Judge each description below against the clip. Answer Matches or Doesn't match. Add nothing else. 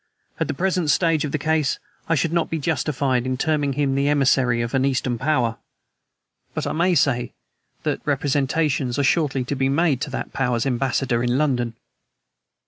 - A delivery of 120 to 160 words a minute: Doesn't match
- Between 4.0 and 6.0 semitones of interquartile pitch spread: Doesn't match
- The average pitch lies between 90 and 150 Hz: Matches